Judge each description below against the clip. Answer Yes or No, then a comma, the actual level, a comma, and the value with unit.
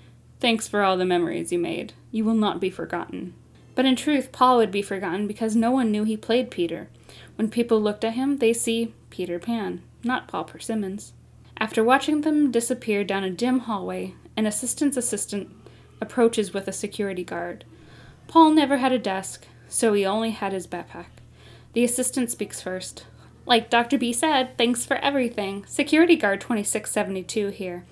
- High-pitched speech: Yes, high, 225 Hz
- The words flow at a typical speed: Yes, average, 170 wpm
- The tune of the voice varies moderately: Yes, average, 4.2 semitones